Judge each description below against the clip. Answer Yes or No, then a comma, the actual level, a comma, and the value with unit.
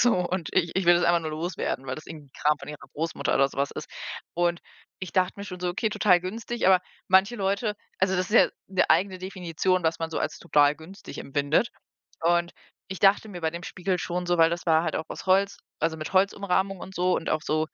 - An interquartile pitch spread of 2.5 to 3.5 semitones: Yes, average, 2.8 semitones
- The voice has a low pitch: No, medium, 175 Hz